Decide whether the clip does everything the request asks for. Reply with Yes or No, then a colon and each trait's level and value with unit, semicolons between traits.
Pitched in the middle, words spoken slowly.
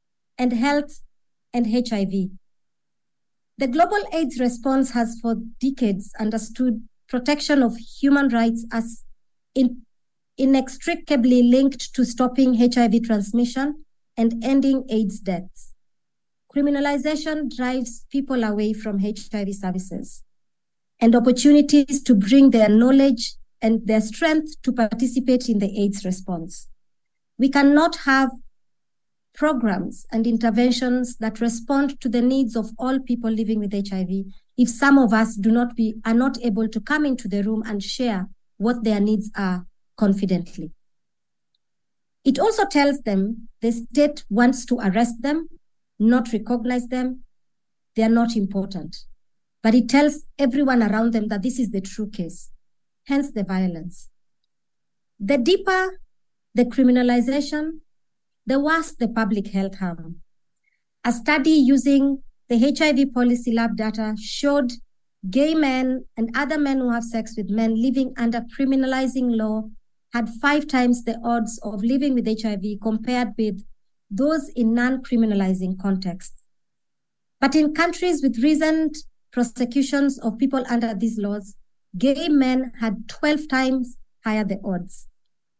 No: high, 240 Hz; slow, 130 wpm